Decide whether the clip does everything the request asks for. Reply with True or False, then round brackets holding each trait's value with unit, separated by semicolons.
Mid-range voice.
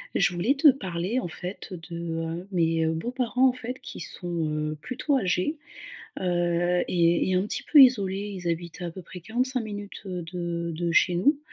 True (180 Hz)